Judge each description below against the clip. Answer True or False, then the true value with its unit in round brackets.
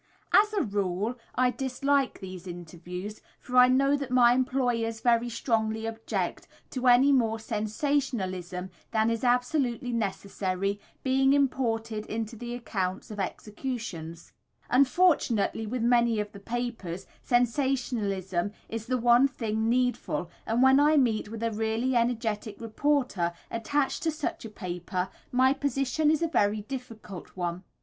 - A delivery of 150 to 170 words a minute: False (140 wpm)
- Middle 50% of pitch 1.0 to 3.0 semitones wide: False (3.8 semitones)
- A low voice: False (230 Hz)